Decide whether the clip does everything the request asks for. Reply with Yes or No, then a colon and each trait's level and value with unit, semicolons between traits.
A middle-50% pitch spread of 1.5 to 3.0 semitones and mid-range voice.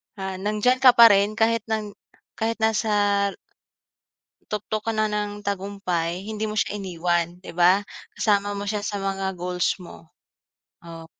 No: narrow, 2.4 semitones; high, 205 Hz